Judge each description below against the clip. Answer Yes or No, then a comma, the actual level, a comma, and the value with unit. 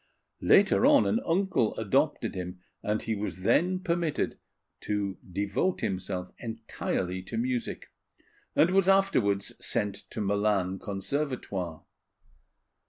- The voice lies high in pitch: No, low, 105 Hz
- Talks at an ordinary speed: No, slow, 110 wpm